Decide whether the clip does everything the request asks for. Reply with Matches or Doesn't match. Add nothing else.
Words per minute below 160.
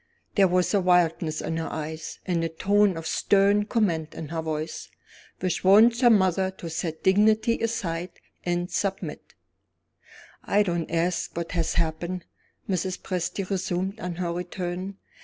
Matches